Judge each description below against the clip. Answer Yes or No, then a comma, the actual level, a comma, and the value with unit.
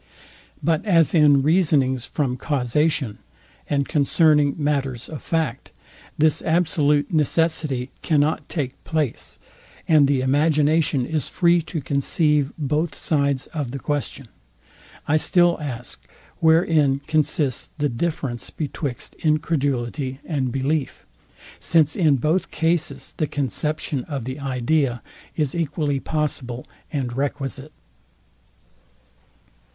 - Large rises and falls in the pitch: No, average, 2.8 semitones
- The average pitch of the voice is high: No, medium, 145 Hz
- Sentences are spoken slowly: Yes, slow, 110 wpm